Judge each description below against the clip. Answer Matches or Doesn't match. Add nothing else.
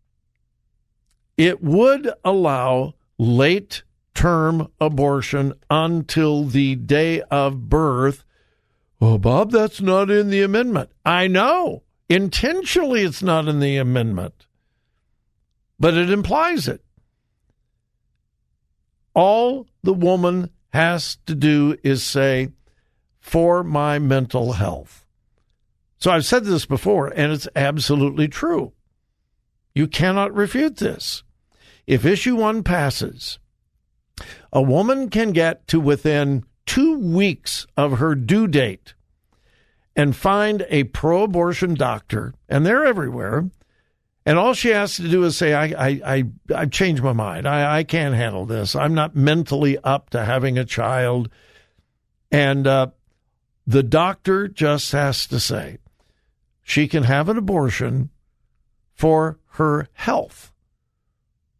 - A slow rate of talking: Matches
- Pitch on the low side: Doesn't match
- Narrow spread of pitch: Doesn't match